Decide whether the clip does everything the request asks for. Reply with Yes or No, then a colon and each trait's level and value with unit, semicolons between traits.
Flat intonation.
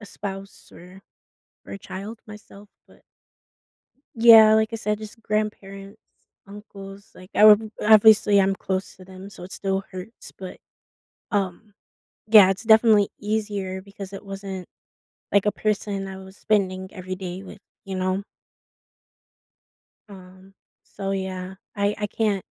Yes: narrow, 1.9 semitones